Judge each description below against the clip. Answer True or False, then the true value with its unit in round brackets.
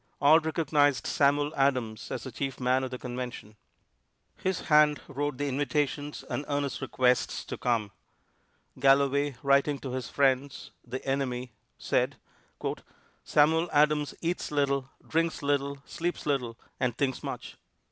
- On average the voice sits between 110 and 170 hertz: True (140 Hz)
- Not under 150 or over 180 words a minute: False (135 wpm)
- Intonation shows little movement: True (2.2 semitones)